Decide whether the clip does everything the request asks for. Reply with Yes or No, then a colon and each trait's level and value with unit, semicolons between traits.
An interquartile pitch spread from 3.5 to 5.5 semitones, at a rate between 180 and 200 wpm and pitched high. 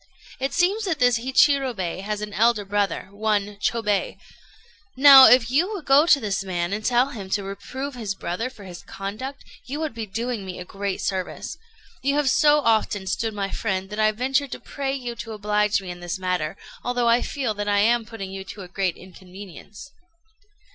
Yes: average, 4.8 semitones; average, 195 wpm; high, 215 Hz